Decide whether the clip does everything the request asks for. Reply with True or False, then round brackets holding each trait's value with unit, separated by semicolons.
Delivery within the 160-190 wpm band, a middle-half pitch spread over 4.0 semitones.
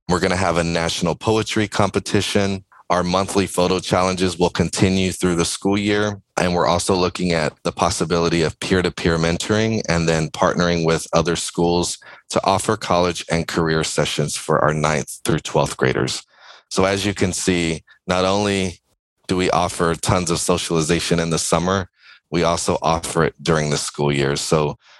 False (175 wpm; 2.6 semitones)